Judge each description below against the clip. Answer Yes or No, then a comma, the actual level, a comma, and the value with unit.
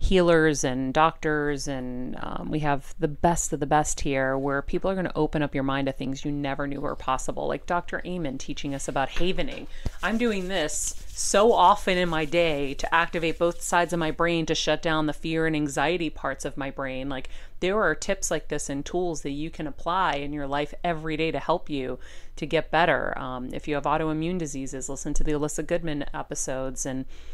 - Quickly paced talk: Yes, fast, 215 wpm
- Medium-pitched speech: Yes, medium, 150 Hz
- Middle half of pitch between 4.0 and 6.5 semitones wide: No, average, 3.3 semitones